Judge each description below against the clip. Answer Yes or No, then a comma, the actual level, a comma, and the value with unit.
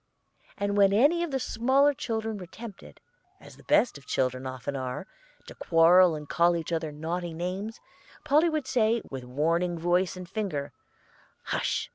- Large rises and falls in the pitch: Yes, wide, 5.9 semitones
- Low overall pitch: No, medium, 180 Hz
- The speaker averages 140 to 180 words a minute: Yes, average, 165 wpm